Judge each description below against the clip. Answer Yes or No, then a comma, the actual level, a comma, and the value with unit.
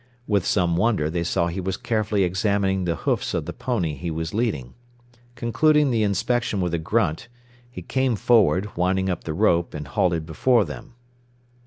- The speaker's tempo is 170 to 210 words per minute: Yes, average, 175 wpm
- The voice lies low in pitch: Yes, very low, 95 Hz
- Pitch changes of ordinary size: Yes, average, 5.0 semitones